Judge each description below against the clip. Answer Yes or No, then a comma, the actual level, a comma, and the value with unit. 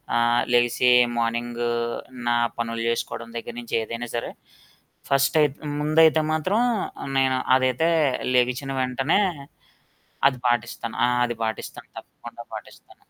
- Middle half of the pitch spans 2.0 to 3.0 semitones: Yes, narrow, 2.5 semitones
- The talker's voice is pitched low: Yes, low, 120 Hz